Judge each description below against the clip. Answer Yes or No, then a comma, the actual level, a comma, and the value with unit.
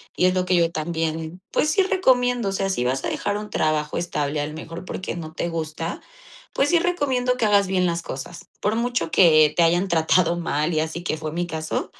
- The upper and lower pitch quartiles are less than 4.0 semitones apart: No, average, 4.3 semitones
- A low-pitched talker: No, medium, 170 Hz